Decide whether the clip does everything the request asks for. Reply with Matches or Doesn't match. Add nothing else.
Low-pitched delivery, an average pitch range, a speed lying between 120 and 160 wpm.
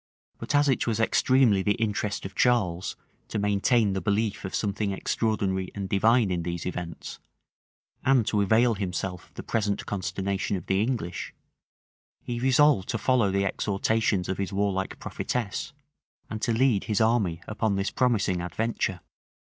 Matches